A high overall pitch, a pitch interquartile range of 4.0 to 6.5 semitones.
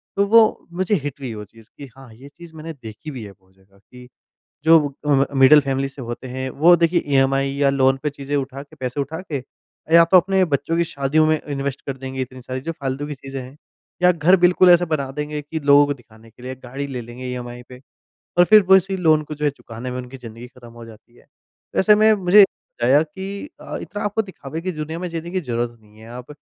No: medium, 140 Hz; average, 4.6 semitones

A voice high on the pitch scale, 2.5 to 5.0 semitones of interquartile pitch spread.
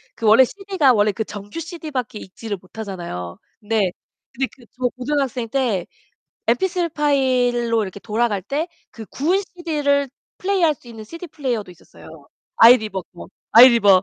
No: high, 240 Hz; wide, 5.5 semitones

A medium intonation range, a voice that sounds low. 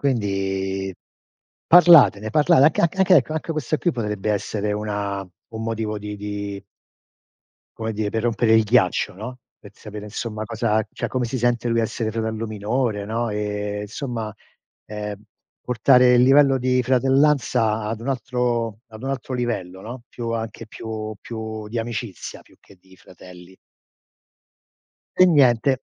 Yes: average, 3.1 semitones; low, 110 Hz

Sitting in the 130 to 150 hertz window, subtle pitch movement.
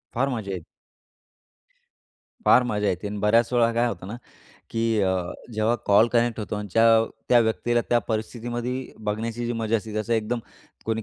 No: low, 115 Hz; narrow, 2.1 semitones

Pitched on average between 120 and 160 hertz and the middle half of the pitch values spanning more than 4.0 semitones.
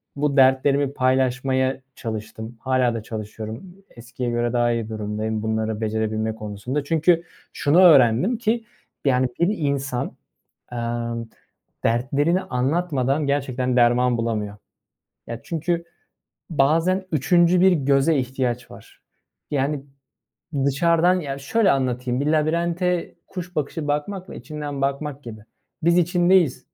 Yes: low, 135 Hz; average, 5.2 semitones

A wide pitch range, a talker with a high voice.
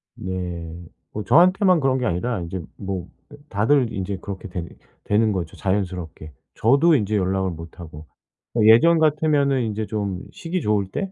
No: wide, 6.7 semitones; low, 100 Hz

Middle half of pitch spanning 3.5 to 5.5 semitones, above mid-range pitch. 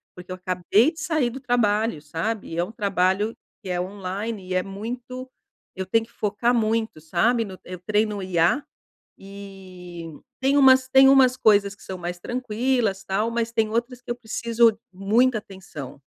Yes: average, 4.2 semitones; high, 210 Hz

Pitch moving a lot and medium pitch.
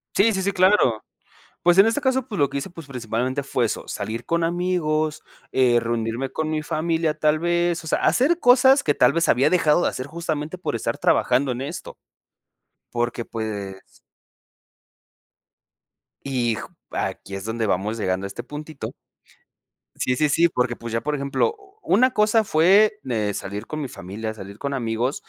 Yes: wide, 6.8 semitones; medium, 145 Hz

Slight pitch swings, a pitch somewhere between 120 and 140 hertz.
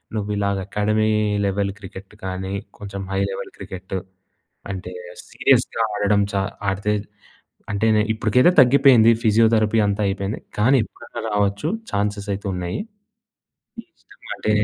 No: narrow, 1.7 semitones; low, 100 Hz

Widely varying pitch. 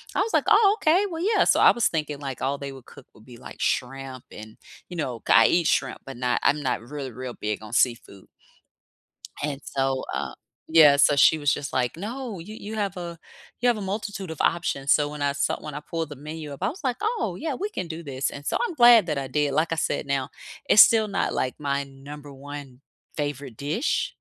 Yes: wide, 6.3 semitones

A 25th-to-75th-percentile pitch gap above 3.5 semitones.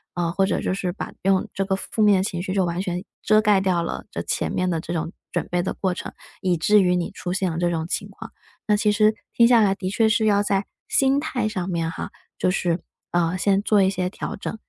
No: average, 2.8 semitones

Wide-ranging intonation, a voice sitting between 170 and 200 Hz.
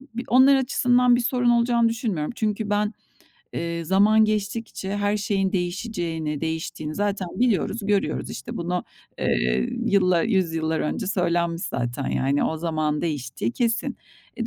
Yes: wide, 5.7 semitones; high, 195 Hz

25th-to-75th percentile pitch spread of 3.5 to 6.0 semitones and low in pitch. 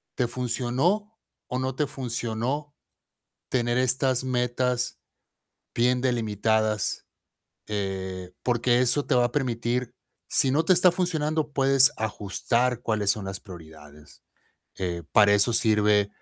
Yes: average, 3.8 semitones; low, 120 Hz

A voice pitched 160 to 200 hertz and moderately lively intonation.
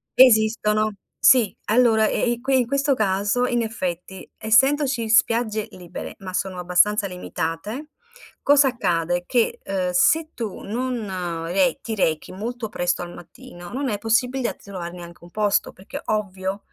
No: high, 215 Hz; average, 4.9 semitones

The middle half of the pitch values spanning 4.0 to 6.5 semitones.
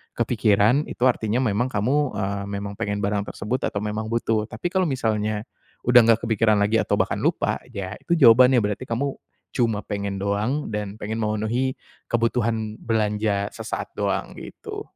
No: average, 2.8 semitones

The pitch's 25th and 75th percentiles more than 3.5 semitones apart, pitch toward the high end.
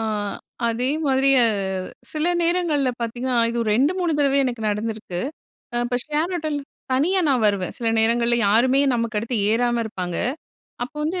Yes: average, 4.5 semitones; high, 245 Hz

